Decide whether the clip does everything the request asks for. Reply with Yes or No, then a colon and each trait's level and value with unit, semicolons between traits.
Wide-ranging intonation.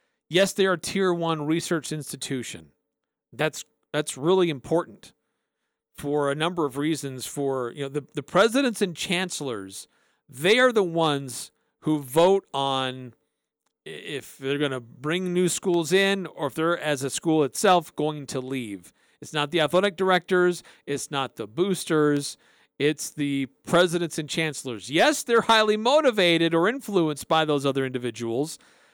No: average, 4.6 semitones